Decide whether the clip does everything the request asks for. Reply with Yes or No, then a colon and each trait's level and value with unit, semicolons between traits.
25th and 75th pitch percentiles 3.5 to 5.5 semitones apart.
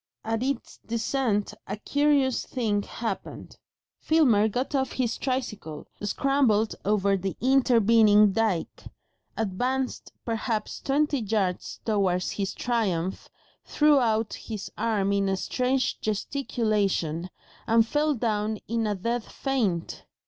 Yes: average, 4.0 semitones